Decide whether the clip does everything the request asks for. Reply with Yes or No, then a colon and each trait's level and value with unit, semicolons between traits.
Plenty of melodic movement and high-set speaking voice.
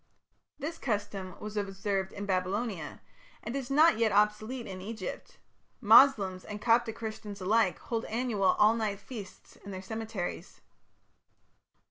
No: average, 2.8 semitones; high, 210 Hz